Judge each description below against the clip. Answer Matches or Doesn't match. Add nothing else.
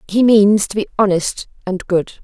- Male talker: Doesn't match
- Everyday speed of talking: Matches